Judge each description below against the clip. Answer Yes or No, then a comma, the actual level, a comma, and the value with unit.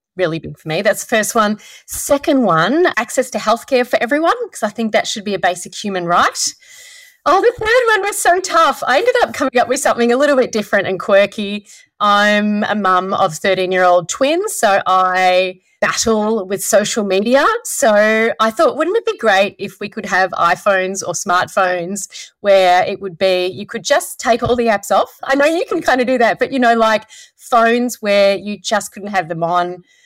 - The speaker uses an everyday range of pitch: No, wide, 6.0 semitones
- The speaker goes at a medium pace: No, fast, 210 wpm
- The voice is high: Yes, high, 215 Hz